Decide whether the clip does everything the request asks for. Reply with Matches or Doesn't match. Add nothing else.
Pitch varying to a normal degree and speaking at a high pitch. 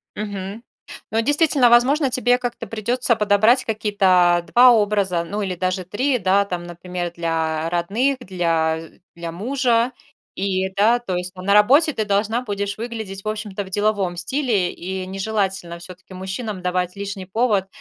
Matches